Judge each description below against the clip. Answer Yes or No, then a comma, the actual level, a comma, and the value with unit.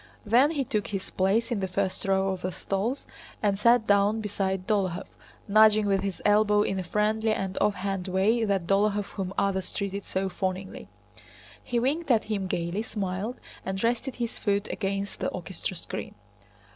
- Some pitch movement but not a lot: No, narrow, 2.1 semitones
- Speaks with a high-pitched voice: Yes, high, 200 Hz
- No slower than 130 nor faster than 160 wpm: No, average, 170 wpm